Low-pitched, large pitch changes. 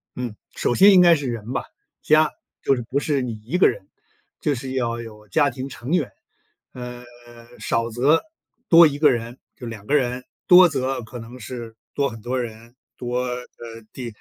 No: low, 125 Hz; average, 3.4 semitones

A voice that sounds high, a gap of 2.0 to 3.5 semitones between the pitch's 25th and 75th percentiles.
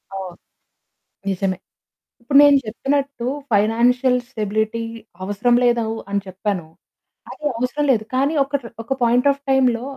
No: high, 235 Hz; average, 4.1 semitones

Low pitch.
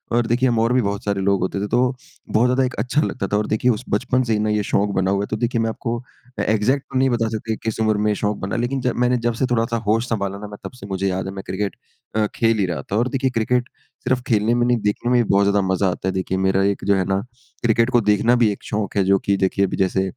Yes: low, 110 Hz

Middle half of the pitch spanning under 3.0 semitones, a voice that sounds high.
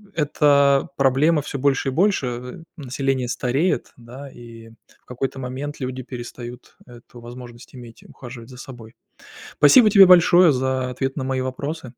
No: narrow, 2.5 semitones; low, 130 Hz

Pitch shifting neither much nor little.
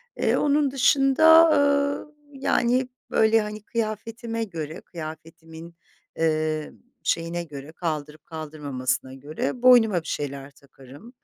No: wide, 8.0 semitones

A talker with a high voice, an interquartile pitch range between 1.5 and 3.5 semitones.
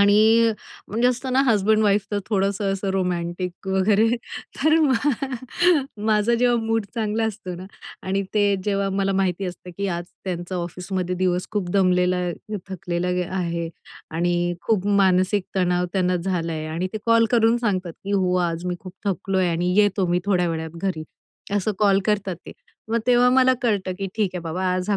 Yes: high, 195 Hz; average, 2.8 semitones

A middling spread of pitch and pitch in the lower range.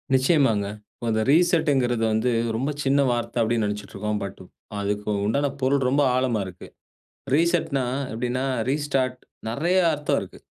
Yes: average, 4.4 semitones; low, 130 Hz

